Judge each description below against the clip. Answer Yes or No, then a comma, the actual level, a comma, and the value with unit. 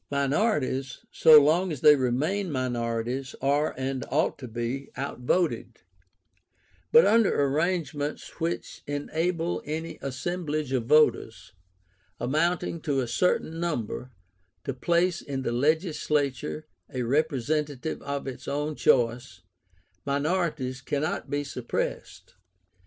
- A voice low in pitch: No, medium, 145 Hz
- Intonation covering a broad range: No, average, 3.6 semitones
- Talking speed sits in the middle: No, slow, 110 wpm